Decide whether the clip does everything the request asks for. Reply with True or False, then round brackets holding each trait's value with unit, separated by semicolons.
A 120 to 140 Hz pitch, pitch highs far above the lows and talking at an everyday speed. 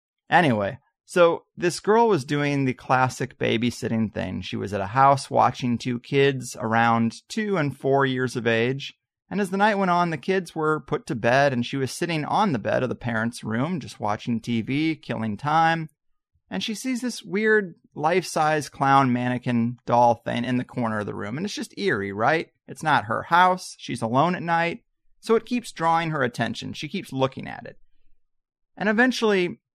True (135 Hz; 6.5 semitones; 195 wpm)